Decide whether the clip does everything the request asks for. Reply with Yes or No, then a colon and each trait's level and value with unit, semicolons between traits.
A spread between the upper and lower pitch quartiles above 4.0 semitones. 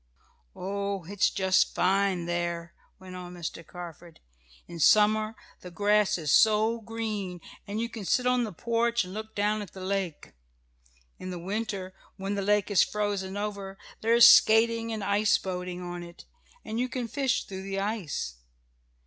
No: average, 3.1 semitones